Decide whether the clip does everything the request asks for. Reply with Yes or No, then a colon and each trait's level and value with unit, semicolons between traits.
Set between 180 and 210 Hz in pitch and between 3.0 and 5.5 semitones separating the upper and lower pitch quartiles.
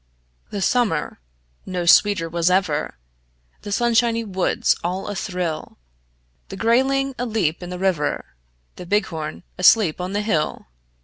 Yes: high, 190 Hz; average, 4.5 semitones